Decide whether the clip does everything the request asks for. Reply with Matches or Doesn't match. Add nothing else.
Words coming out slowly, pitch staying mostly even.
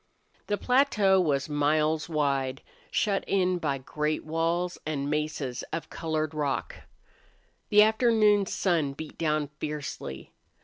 Doesn't match